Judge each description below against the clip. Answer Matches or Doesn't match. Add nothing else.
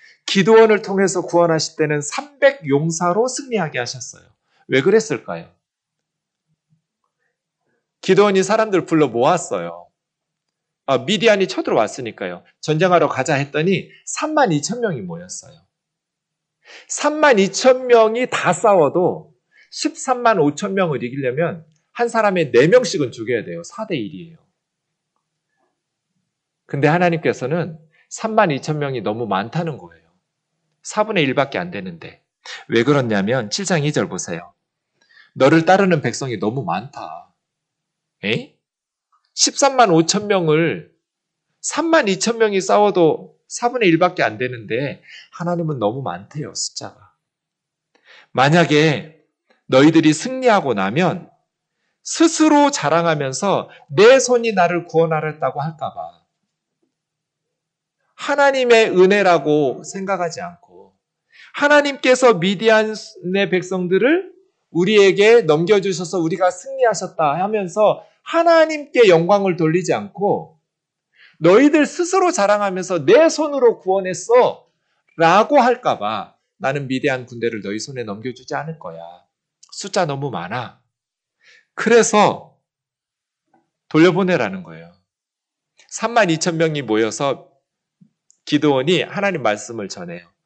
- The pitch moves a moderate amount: Doesn't match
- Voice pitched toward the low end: Doesn't match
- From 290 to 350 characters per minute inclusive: Doesn't match